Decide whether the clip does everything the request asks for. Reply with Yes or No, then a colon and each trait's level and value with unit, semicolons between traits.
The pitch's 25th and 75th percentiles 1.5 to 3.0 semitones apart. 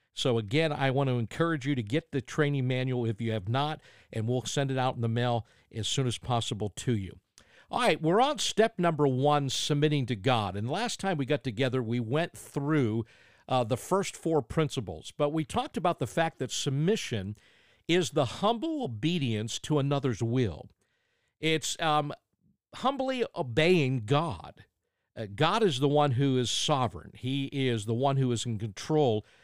No: average, 4.9 semitones